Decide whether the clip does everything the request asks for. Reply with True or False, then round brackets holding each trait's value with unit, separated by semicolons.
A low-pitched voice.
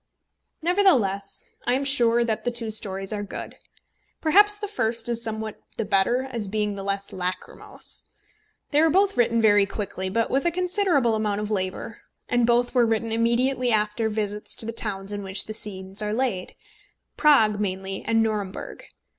False (220 Hz)